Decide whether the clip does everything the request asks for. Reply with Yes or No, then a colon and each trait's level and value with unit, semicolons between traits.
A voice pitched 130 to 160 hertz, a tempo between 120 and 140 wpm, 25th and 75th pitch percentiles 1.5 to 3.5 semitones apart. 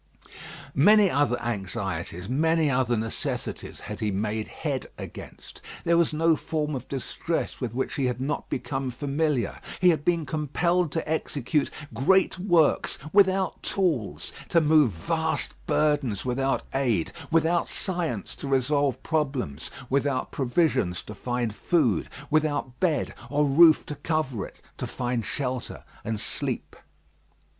No: medium, 140 Hz; slow, 135 wpm; average, 4.9 semitones